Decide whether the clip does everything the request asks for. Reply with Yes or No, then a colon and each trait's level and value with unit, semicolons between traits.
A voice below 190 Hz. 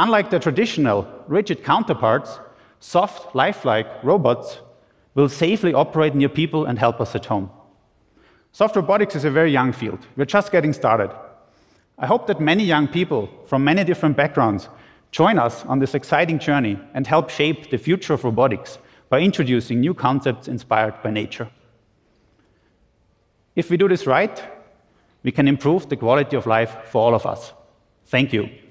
Yes: medium, 140 Hz